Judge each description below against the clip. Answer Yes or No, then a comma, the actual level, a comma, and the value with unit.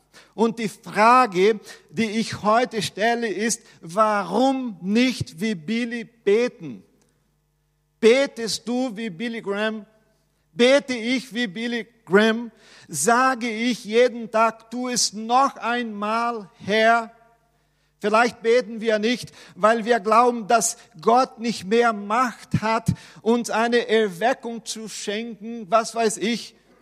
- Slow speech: Yes, slow, 120 wpm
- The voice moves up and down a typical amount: No, narrow, 1.9 semitones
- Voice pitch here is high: Yes, high, 225 Hz